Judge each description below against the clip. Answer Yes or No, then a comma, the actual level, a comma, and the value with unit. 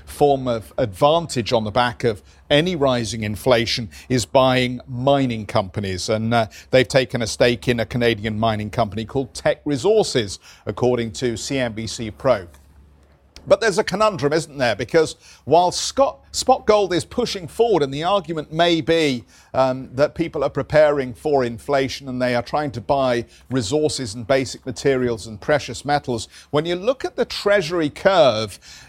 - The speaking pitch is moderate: No, low, 130 Hz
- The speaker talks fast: No, average, 160 wpm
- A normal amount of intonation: Yes, average, 4.6 semitones